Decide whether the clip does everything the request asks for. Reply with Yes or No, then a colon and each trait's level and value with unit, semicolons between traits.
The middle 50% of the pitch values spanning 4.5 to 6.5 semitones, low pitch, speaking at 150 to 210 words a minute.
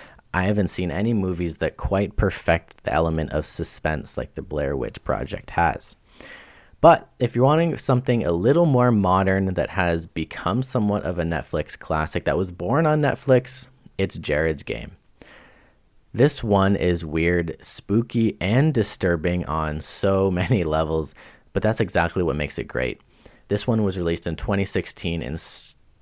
Yes: average, 5.2 semitones; very low, 95 Hz; average, 155 wpm